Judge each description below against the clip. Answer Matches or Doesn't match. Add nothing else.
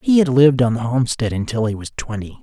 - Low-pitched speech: Matches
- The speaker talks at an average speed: Doesn't match